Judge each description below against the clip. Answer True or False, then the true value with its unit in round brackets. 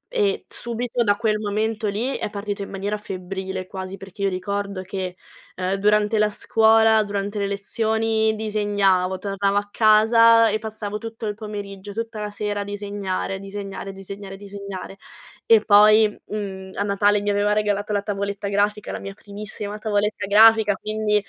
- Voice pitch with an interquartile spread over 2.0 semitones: False (1.4 semitones)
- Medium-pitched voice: False (205 Hz)